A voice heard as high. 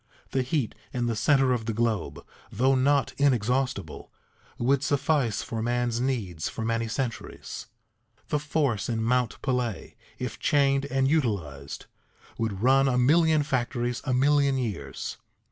No: low, 125 Hz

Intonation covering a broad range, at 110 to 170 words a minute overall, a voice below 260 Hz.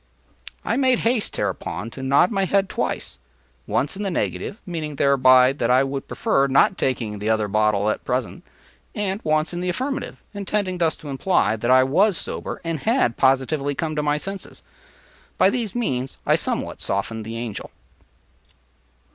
Yes: wide, 7.9 semitones; average, 165 wpm; medium, 140 Hz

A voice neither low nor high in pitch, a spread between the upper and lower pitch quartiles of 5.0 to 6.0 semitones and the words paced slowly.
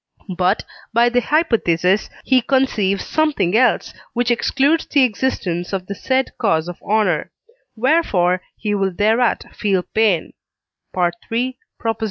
No: high, 220 Hz; wide, 5.4 semitones; slow, 125 wpm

